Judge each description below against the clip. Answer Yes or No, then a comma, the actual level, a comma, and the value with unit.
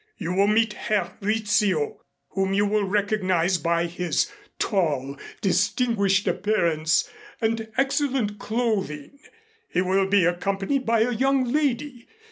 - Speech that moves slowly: Yes, slow, 120 wpm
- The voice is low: No, high, 205 Hz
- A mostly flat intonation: No, average, 3.8 semitones